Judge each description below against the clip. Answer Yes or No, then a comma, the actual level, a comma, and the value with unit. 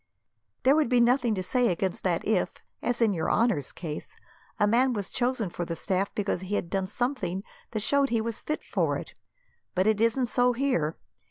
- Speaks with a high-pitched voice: Yes, high, 220 Hz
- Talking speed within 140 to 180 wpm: No, fast, 205 wpm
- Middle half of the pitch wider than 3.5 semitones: Yes, average, 4.7 semitones